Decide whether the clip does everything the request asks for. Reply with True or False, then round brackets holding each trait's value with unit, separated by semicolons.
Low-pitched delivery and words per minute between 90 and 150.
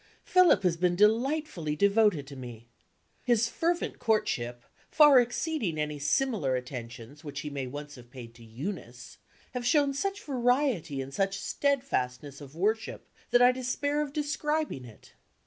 False (190 Hz; 145 wpm)